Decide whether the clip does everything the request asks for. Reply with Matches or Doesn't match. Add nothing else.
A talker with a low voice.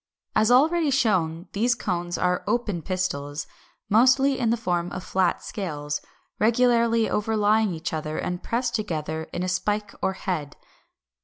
Doesn't match